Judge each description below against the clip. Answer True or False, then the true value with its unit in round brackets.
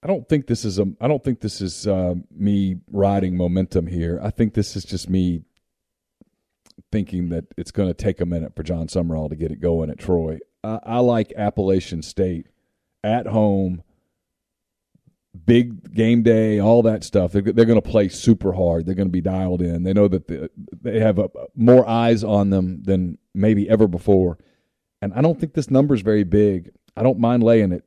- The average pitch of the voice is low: True (100 Hz)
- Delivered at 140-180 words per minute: False (200 wpm)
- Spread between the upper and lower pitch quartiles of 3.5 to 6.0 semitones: True (3.9 semitones)